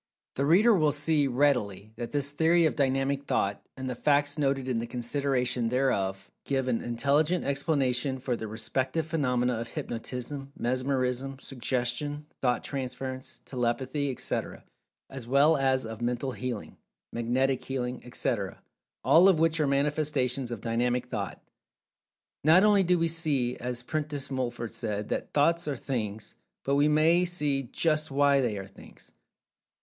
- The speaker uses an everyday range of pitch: Yes, average, 3.1 semitones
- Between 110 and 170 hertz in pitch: Yes, low, 135 Hz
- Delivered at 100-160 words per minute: Yes, average, 150 wpm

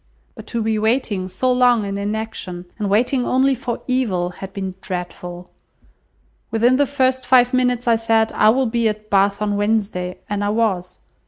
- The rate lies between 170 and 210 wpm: Yes, average, 175 wpm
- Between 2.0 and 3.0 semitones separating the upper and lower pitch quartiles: No, average, 3.8 semitones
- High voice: Yes, high, 220 Hz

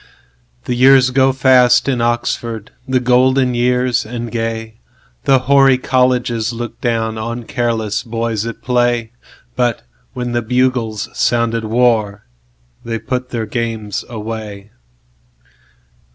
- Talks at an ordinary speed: No, slow, 100 wpm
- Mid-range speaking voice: No, low, 120 Hz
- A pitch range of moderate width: No, narrow, 2.0 semitones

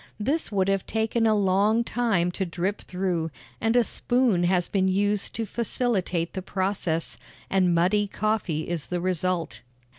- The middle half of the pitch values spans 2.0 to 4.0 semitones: Yes, average, 3.5 semitones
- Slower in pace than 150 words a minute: No, average, 155 wpm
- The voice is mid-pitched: No, high, 195 Hz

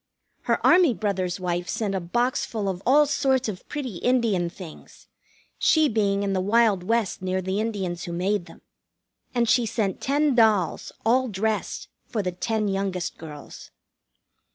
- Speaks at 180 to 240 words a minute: No, average, 160 wpm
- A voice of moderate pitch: No, high, 205 Hz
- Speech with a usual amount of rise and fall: Yes, average, 4.3 semitones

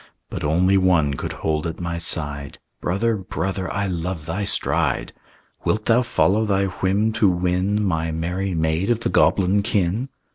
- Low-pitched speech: Yes, very low, 95 Hz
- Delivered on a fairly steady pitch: No, average, 3.5 semitones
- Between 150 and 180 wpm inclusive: Yes, average, 160 wpm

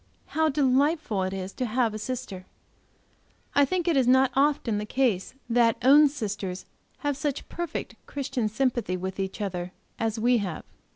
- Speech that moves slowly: No, average, 165 wpm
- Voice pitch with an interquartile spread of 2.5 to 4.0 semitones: No, average, 5.3 semitones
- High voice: Yes, high, 245 Hz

